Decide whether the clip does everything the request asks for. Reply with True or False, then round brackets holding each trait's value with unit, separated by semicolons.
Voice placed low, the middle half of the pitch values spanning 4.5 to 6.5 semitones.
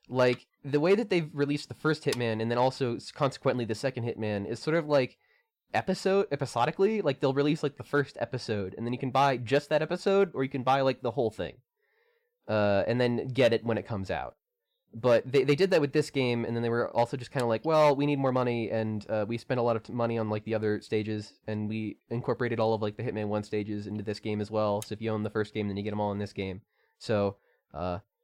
True (120 Hz; 4.9 semitones)